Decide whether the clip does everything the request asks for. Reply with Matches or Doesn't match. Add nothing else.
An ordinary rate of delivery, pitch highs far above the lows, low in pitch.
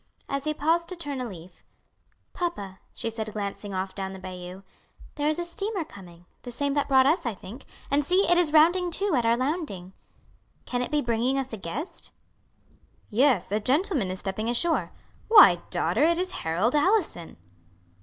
Doesn't match